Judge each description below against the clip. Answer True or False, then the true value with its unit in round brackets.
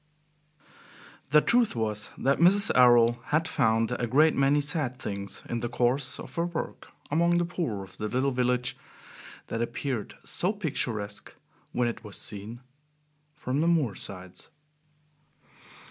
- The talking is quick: False (145 wpm)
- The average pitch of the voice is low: True (125 Hz)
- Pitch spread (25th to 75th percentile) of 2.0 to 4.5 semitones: False (5.1 semitones)